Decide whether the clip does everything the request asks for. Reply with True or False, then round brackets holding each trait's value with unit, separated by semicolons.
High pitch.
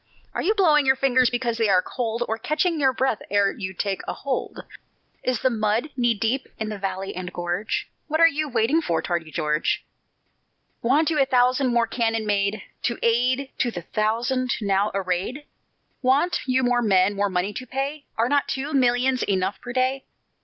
True (240 Hz)